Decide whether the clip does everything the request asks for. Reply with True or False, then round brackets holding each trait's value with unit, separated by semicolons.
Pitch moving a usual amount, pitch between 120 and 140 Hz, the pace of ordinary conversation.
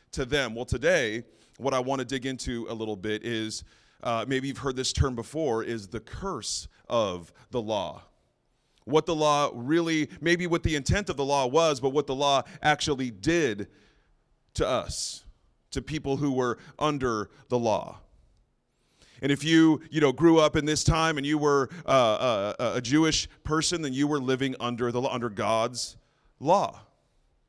True (4.2 semitones; 135 Hz; 175 wpm)